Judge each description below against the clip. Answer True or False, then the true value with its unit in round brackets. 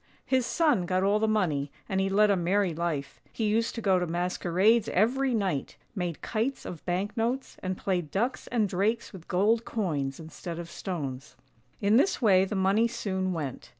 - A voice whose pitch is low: False (190 Hz)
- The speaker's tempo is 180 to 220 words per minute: True (185 wpm)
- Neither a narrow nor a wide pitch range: True (4.0 semitones)